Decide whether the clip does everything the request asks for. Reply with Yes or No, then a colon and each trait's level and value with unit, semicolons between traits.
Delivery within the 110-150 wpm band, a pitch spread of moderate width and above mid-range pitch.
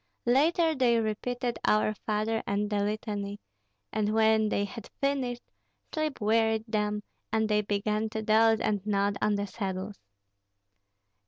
No: average, 140 wpm; narrow, 1.6 semitones; high, 215 Hz